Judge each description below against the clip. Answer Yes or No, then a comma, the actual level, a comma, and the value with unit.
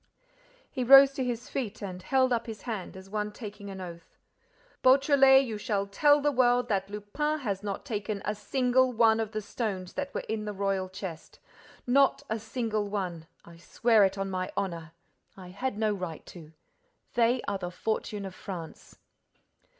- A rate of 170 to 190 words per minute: Yes, average, 180 wpm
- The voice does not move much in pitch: No, average, 4.3 semitones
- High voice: Yes, high, 210 Hz